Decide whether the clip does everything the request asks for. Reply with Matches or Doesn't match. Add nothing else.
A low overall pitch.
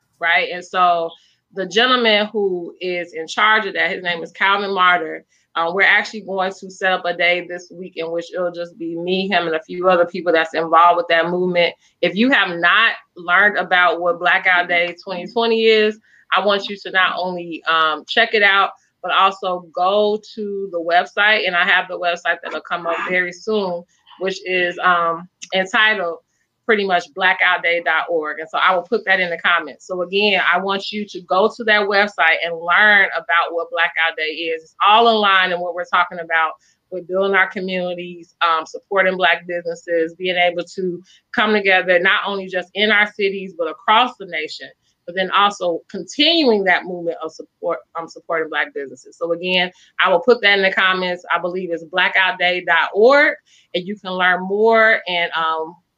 Doesn't match